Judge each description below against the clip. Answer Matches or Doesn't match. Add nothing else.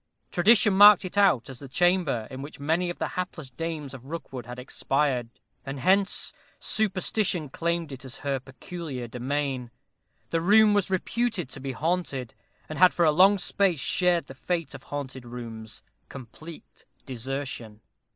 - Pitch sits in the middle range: Matches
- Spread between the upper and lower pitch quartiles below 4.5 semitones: Doesn't match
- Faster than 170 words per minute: Doesn't match